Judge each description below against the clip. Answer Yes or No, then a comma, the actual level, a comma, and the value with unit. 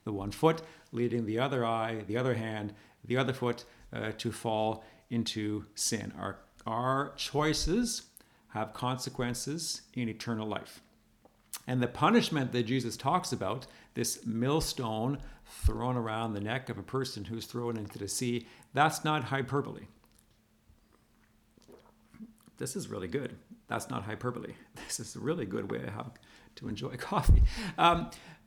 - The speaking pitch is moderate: No, low, 120 Hz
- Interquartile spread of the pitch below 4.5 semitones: Yes, average, 3.4 semitones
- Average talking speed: Yes, average, 145 wpm